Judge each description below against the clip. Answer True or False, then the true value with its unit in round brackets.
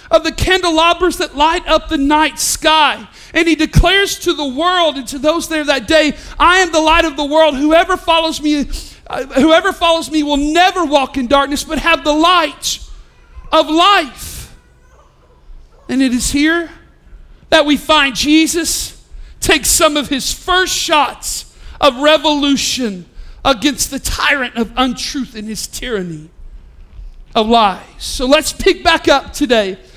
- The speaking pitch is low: False (305 Hz)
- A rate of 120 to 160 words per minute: True (155 wpm)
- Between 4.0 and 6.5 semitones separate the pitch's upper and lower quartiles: False (3.4 semitones)